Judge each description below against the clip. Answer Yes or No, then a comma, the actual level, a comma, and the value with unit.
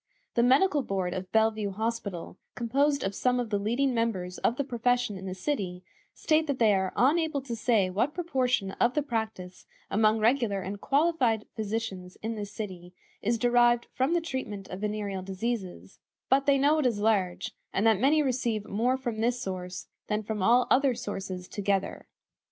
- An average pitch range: Yes, average, 4.5 semitones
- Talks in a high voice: Yes, high, 225 Hz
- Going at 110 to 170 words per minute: No, average, 180 wpm